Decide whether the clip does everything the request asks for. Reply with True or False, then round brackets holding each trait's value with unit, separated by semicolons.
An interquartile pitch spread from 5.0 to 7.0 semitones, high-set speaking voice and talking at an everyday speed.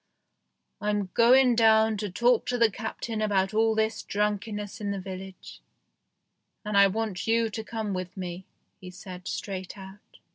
False (2.6 semitones; 210 Hz; 155 wpm)